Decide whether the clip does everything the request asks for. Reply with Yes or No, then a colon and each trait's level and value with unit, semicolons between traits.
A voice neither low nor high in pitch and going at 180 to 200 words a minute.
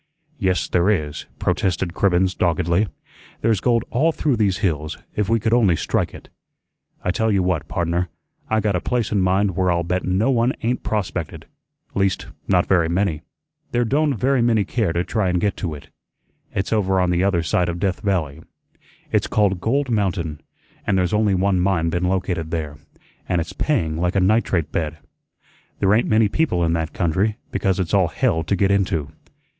No: very low, 95 Hz; average, 190 wpm